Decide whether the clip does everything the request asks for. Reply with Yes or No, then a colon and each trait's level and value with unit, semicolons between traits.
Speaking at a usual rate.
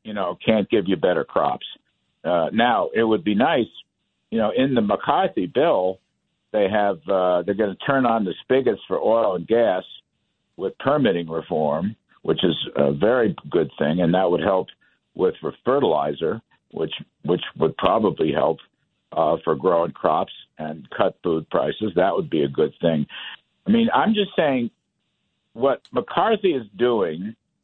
Yes: average, 165 wpm